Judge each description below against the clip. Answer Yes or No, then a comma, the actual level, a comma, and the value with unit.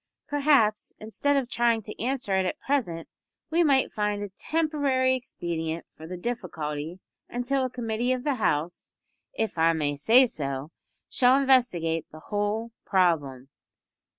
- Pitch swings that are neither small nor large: No, wide, 7.7 semitones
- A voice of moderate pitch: No, high, 220 Hz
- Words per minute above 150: No, average, 145 wpm